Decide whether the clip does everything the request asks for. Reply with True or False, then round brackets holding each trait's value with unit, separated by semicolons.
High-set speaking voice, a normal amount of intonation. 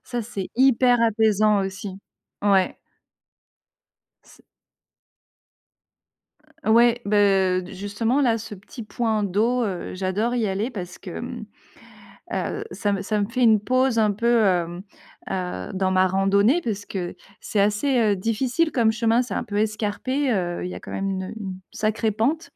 True (215 Hz; 3.3 semitones)